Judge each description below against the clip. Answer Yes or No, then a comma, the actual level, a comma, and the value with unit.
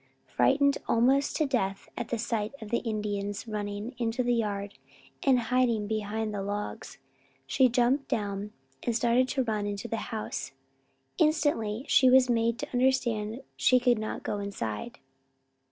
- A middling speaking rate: Yes, average, 155 wpm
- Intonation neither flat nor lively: Yes, average, 3.3 semitones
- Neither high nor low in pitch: No, high, 230 Hz